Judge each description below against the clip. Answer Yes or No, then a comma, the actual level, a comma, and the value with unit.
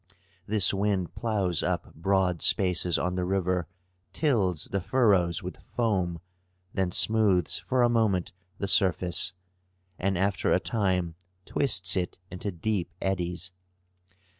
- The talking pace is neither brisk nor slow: No, slow, 125 wpm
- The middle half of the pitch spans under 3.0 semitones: Yes, narrow, 2.5 semitones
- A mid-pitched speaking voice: No, very low, 95 Hz